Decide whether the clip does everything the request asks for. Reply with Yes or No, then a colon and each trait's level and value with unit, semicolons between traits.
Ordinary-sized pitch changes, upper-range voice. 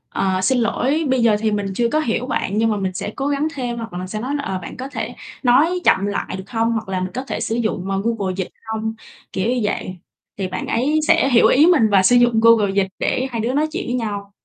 Yes: average, 4.1 semitones; high, 225 Hz